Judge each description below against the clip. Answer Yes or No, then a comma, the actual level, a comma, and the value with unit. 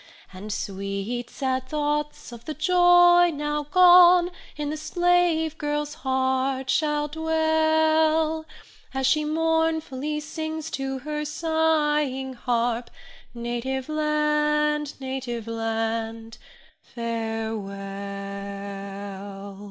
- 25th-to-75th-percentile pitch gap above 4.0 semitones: Yes, wide, 5.4 semitones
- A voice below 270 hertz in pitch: No, very high, 295 Hz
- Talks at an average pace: No, slow, 90 wpm